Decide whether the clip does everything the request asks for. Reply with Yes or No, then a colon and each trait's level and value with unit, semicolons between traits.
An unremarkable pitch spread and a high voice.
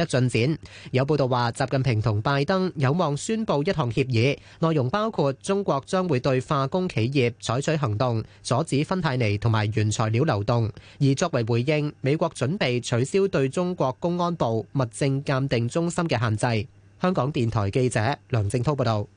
No: average, 4.9 semitones; low, 135 Hz